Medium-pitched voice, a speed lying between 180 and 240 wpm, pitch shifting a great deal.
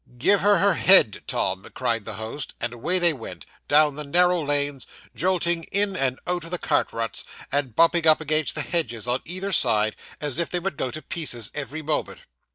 Yes: medium, 150 Hz; average, 200 wpm; wide, 6.1 semitones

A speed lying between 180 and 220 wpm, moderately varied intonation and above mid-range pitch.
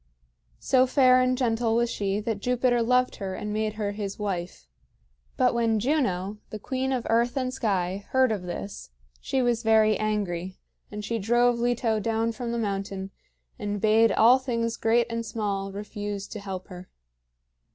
No: average, 170 wpm; average, 3.0 semitones; high, 220 Hz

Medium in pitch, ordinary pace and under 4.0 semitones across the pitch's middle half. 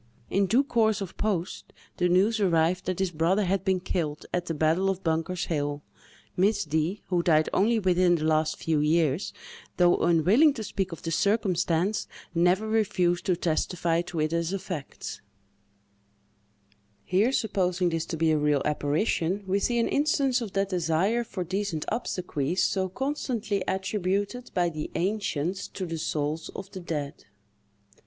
Yes: medium, 180 Hz; average, 160 wpm; average, 3.6 semitones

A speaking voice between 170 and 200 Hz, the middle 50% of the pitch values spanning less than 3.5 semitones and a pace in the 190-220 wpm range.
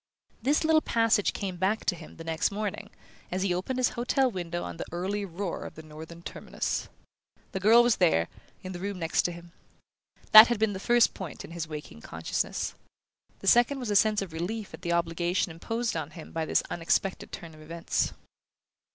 No: medium, 185 Hz; average, 4.6 semitones; average, 200 wpm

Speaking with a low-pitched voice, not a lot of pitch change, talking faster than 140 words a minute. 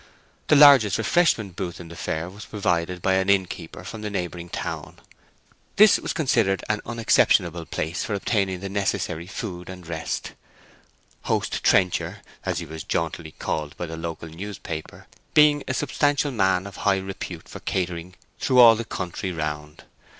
No: very low, 95 Hz; average, 4.3 semitones; average, 160 wpm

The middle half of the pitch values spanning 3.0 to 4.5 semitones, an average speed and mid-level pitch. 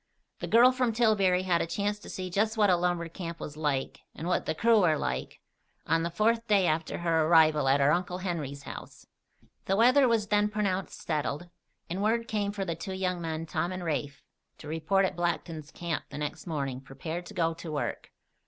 No: average, 4.2 semitones; fast, 210 wpm; medium, 175 Hz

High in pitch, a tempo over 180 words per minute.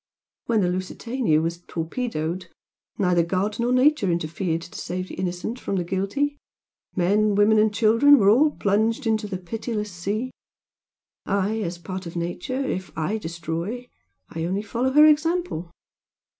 No: high, 200 Hz; average, 155 wpm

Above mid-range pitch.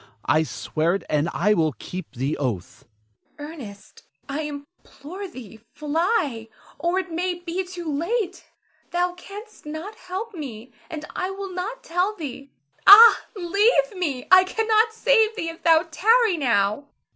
Yes: very high, 340 Hz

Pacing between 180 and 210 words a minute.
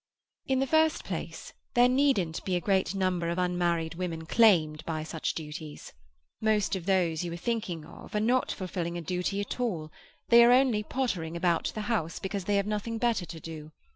Yes: average, 195 wpm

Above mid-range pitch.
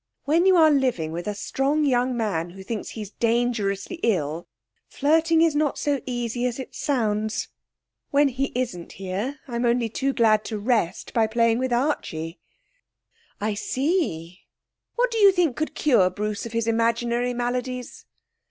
Yes: high, 240 Hz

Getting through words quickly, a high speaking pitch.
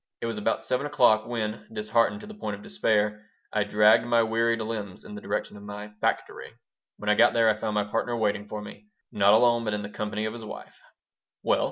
No: fast, 225 wpm; low, 110 Hz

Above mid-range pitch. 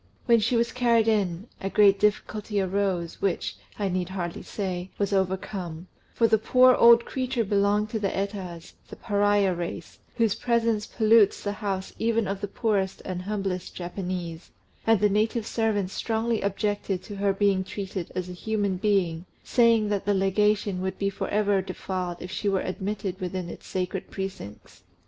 Yes: high, 200 Hz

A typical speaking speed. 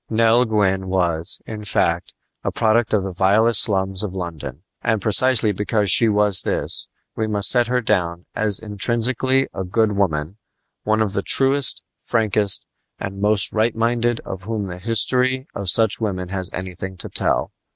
Yes: average, 165 wpm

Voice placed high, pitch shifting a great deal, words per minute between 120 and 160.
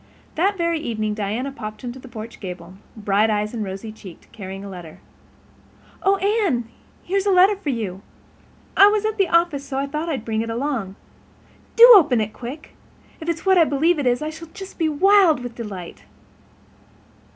No: very high, 270 Hz; wide, 8.0 semitones; average, 190 wpm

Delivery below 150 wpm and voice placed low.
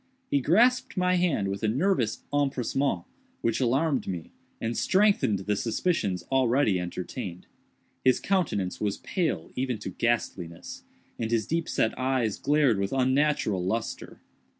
Yes: slow, 135 wpm; low, 125 Hz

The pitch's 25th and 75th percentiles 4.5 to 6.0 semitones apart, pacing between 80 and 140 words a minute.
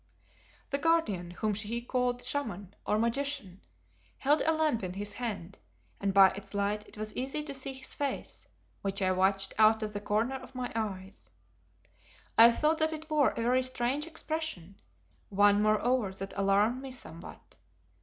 No: average, 5.1 semitones; average, 165 wpm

